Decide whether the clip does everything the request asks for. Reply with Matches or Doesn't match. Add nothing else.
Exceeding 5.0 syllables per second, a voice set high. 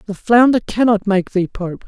Doesn't match